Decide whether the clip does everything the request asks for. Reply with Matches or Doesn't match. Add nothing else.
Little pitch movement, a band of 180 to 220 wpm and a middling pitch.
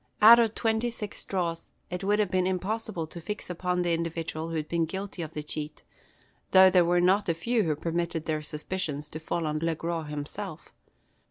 Doesn't match